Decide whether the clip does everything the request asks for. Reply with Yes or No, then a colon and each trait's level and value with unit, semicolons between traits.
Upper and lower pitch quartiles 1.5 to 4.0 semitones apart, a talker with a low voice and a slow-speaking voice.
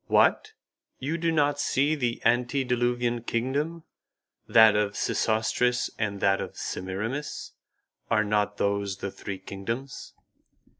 No: average, 4.5 semitones; low, 115 Hz; slow, 115 wpm